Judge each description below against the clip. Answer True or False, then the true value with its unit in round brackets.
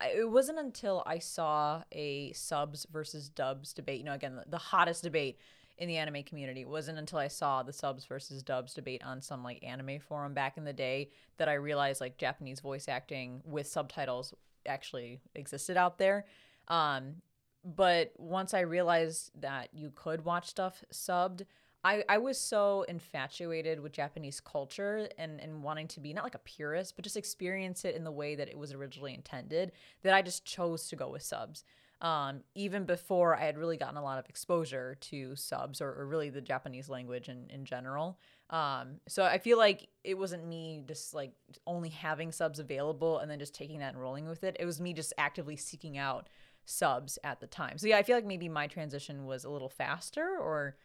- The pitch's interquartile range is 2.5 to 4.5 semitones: True (3.9 semitones)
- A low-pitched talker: False (155 Hz)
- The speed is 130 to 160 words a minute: False (200 wpm)